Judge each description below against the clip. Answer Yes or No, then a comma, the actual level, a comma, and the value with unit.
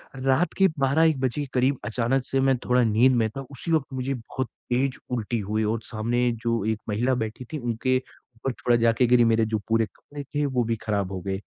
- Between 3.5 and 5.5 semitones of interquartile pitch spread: No, average, 2.9 semitones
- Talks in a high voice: No, low, 125 Hz